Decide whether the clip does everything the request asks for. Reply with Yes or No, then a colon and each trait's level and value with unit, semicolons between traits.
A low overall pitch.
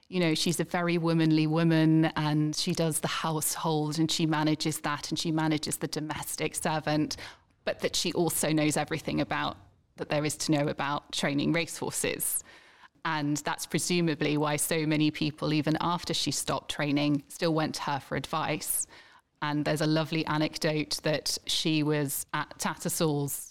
No: medium, 155 Hz